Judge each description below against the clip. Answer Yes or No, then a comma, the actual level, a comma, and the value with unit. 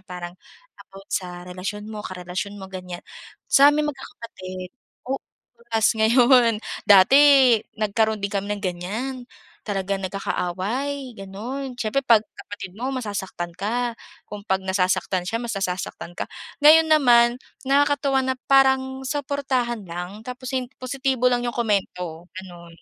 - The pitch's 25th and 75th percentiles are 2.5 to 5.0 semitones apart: No, wide, 5.4 semitones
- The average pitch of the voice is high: Yes, high, 220 Hz